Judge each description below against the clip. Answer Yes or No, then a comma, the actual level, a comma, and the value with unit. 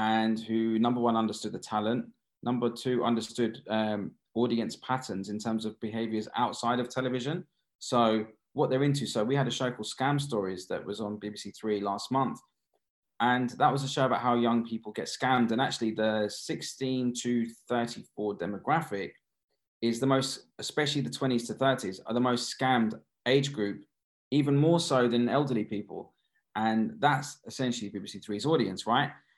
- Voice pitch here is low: Yes, low, 120 Hz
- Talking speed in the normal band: Yes, average, 170 wpm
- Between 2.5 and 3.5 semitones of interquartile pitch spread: Yes, average, 3.1 semitones